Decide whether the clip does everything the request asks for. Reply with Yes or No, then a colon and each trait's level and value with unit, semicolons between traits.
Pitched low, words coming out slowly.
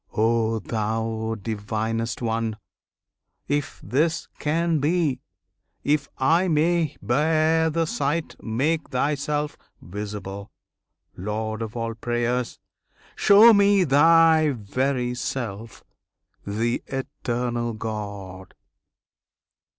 Yes: low, 125 Hz; slow, 90 wpm